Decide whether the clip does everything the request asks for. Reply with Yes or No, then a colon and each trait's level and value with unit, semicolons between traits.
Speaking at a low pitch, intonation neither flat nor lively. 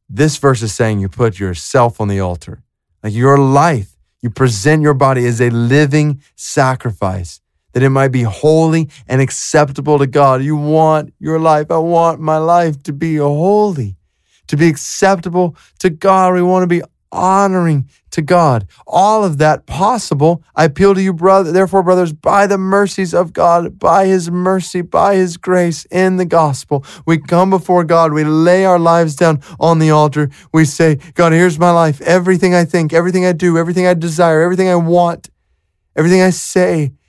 No: medium, 160 Hz; average, 4.5 semitones